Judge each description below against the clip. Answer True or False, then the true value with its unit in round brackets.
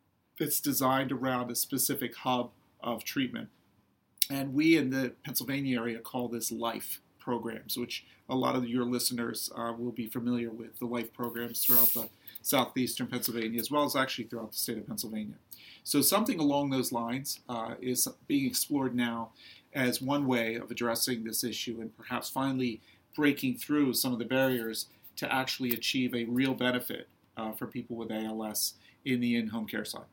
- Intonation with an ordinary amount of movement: False (2.1 semitones)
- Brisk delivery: False (175 wpm)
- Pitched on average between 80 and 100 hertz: False (120 Hz)